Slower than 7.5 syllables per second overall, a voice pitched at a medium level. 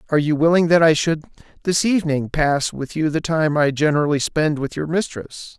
Yes: 5.4 syllables/s; medium, 155 Hz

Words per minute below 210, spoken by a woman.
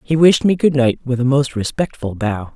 No: fast, 235 wpm; female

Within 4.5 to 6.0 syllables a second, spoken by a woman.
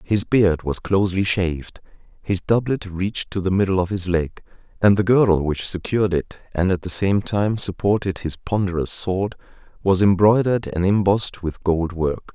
No: 5.0 syllables/s; male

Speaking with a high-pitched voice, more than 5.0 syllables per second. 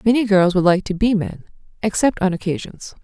Yes: high, 195 Hz; 5.6 syllables/s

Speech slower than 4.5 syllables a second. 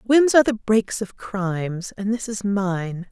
Yes: 4.3 syllables/s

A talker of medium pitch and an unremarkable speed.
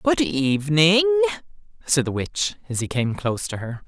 Yes: medium, 170 Hz; average, 170 wpm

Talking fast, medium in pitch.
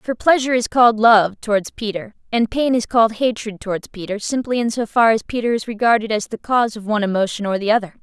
No: fast, 230 wpm; high, 225 Hz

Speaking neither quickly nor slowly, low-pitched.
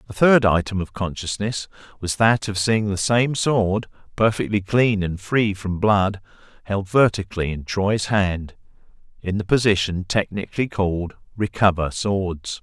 Yes: average, 145 wpm; low, 100 Hz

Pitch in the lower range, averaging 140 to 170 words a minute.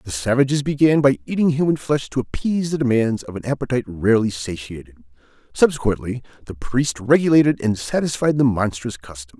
Yes: low, 125 Hz; average, 160 wpm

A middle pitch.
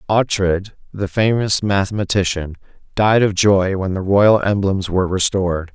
No: low, 100 Hz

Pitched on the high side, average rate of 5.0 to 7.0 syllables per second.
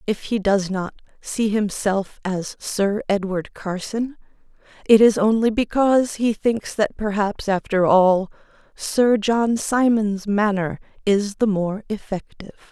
No: high, 210 Hz; 3.9 syllables/s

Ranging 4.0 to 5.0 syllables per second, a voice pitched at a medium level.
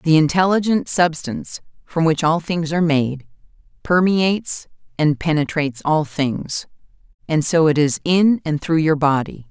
Yes: 4.5 syllables/s; medium, 160 Hz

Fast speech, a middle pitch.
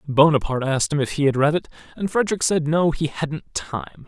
Yes: fast, 220 wpm; medium, 145 Hz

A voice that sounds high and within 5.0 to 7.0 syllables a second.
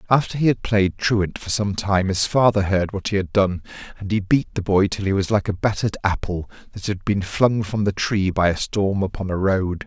No: low, 100 Hz; 5.2 syllables/s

